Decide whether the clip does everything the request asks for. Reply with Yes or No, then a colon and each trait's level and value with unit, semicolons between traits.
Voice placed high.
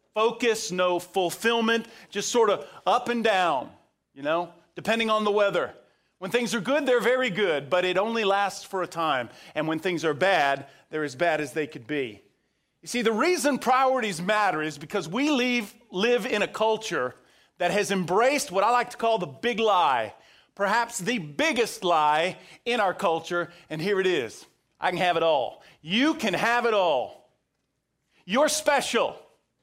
Yes: high, 205 Hz